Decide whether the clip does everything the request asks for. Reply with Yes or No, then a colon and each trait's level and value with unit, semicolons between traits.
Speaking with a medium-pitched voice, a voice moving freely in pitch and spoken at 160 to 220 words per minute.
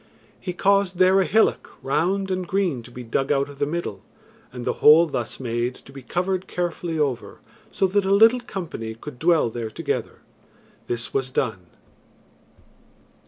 Yes: medium, 160 Hz; wide, 7.0 semitones; average, 165 wpm